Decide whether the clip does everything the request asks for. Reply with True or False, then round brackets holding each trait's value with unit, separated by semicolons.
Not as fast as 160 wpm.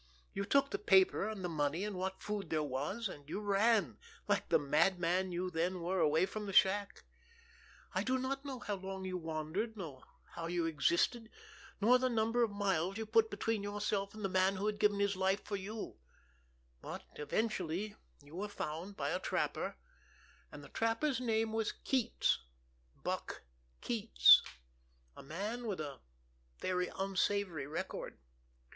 False (165 wpm)